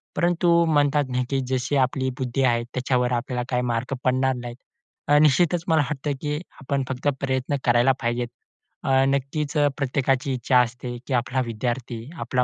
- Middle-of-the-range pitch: No, low, 130 Hz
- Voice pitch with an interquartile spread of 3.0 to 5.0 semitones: No, narrow, 2.6 semitones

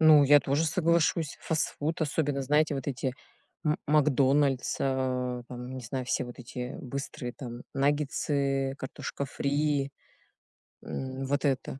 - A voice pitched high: No, medium, 140 Hz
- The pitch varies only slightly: Yes, narrow, 2.2 semitones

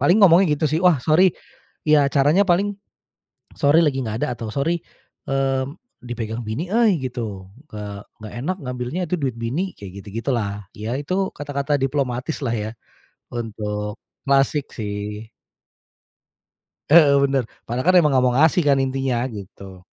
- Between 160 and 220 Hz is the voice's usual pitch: No, low, 135 Hz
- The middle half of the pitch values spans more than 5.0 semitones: Yes, wide, 5.4 semitones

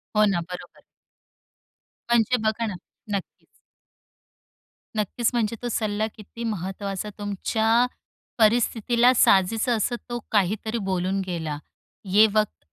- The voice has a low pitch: No, high, 215 Hz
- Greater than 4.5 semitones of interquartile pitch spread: No, average, 2.9 semitones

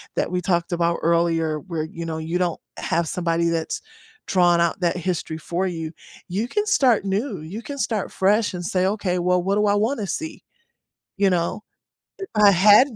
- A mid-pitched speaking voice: Yes, medium, 180 Hz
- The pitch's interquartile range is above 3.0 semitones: Yes, average, 3.4 semitones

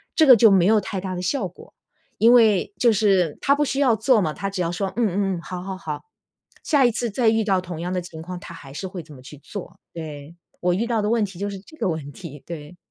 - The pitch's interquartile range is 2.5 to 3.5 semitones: No, average, 4.6 semitones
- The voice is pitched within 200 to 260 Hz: No, high, 190 Hz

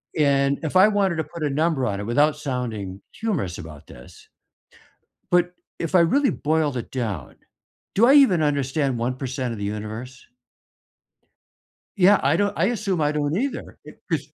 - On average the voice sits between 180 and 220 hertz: No, medium, 145 Hz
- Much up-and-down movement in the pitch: Yes, wide, 6.3 semitones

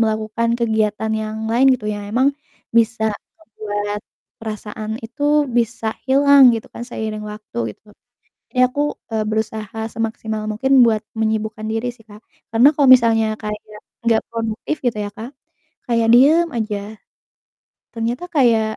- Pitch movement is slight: Yes, narrow, 2.1 semitones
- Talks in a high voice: Yes, high, 225 Hz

